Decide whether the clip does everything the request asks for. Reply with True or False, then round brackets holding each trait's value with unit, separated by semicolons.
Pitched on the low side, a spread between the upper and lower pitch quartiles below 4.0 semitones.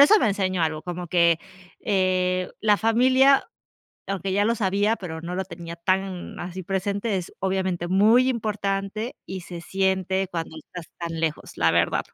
False (190 Hz; 2.7 semitones)